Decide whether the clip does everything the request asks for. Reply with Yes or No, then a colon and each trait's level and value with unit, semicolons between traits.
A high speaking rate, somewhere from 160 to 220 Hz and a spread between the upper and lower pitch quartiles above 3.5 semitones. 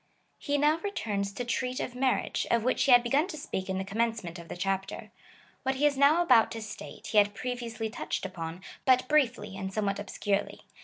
No: fast, 210 wpm; high, 230 Hz; average, 4.9 semitones